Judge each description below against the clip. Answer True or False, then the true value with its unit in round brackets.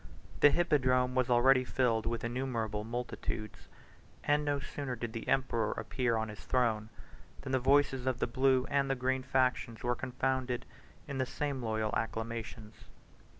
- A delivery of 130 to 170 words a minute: True (155 wpm)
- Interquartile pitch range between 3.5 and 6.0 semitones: False (2.5 semitones)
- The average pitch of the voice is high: False (125 Hz)